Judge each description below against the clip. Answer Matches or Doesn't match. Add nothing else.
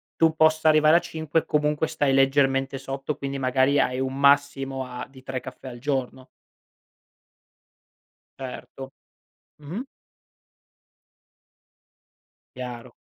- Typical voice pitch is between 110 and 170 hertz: Matches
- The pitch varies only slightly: Matches